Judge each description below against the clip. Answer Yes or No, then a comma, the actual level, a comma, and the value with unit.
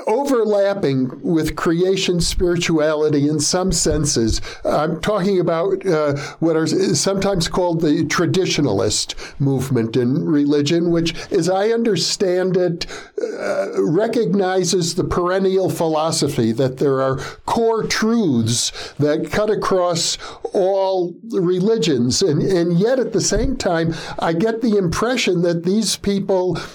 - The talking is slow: Yes, slow, 120 wpm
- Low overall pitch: No, medium, 175 Hz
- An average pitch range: Yes, average, 4.1 semitones